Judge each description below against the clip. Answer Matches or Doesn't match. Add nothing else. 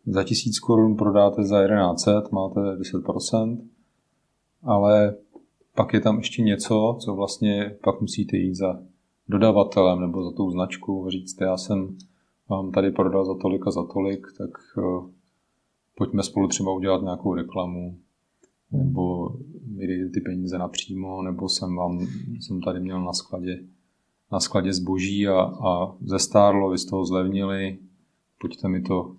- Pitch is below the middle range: Matches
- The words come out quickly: Doesn't match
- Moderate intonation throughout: Doesn't match